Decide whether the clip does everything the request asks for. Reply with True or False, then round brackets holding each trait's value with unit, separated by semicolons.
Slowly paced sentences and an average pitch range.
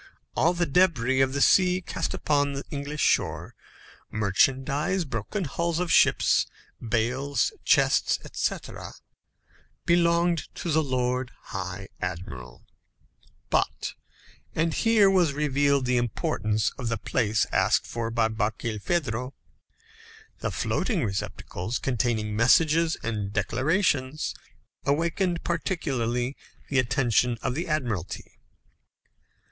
False (110 wpm; 6.3 semitones)